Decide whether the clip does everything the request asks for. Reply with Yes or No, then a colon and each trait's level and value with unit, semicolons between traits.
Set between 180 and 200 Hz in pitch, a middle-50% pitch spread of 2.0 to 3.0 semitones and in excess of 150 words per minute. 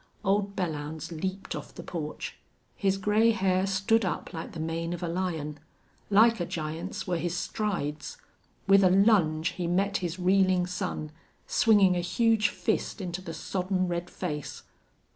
Yes: medium, 185 Hz; average, 2.7 semitones; average, 160 wpm